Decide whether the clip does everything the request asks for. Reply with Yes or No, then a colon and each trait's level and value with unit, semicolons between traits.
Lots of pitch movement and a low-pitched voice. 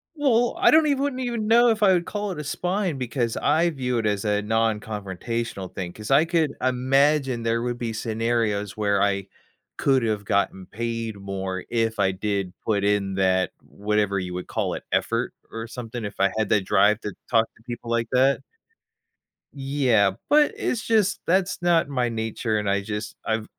Yes: wide, 5.8 semitones; low, 115 Hz